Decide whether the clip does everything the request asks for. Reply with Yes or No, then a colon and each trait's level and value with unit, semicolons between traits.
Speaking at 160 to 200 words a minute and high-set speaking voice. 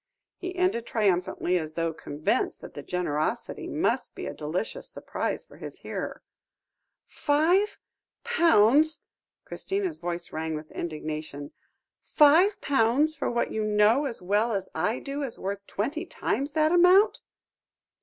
No: slow, 135 wpm; high, 225 Hz